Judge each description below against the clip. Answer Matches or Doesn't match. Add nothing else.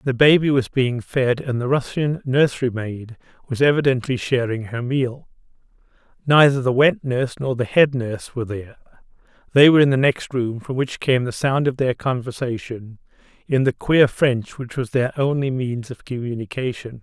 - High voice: Doesn't match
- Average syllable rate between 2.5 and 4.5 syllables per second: Doesn't match